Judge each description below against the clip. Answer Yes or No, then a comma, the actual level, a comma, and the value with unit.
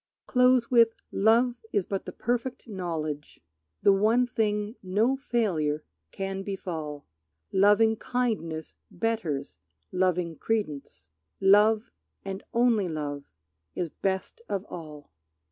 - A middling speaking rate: No, slow, 105 wpm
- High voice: Yes, high, 195 Hz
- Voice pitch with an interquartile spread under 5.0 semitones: No, wide, 5.4 semitones